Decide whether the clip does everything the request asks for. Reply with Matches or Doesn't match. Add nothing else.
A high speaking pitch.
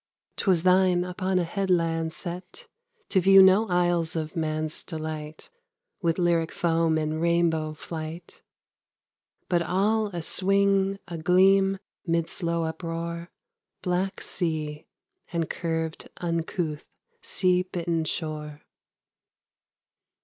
Doesn't match